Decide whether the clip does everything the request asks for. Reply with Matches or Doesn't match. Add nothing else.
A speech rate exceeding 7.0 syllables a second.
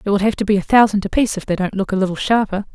Matches